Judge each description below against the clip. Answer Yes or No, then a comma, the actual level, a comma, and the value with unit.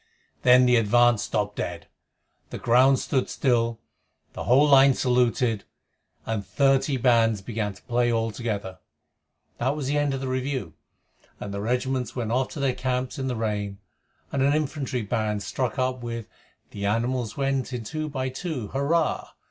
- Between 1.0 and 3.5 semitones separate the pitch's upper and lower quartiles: Yes, average, 3.0 semitones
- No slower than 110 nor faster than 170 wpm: Yes, average, 165 wpm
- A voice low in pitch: Yes, low, 125 Hz